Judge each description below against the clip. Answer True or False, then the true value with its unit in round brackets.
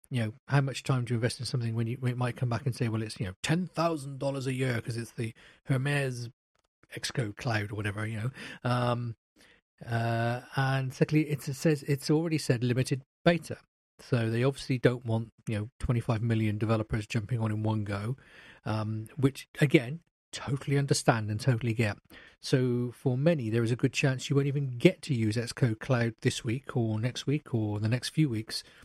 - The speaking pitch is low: True (125 Hz)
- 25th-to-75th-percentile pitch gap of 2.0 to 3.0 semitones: False (3.5 semitones)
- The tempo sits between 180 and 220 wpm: True (200 wpm)